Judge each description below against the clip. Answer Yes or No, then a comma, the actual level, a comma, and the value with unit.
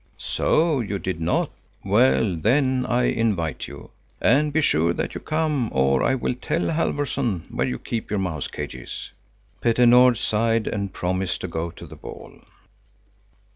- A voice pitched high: No, low, 110 Hz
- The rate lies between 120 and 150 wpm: No, average, 160 wpm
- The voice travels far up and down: Yes, wide, 7.1 semitones